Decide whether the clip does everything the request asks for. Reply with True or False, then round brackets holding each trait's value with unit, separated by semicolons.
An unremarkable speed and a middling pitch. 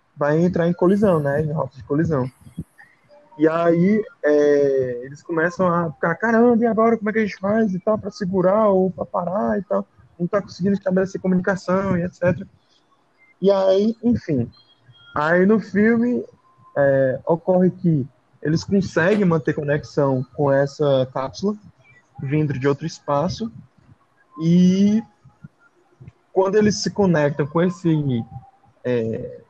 True (140 wpm; 170 Hz)